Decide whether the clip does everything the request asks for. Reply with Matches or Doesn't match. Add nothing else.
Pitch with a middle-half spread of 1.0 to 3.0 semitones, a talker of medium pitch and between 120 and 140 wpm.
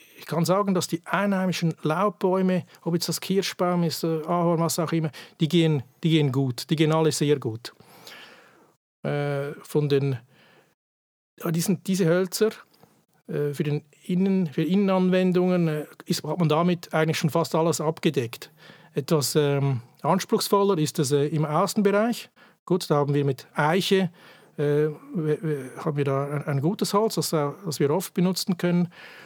Doesn't match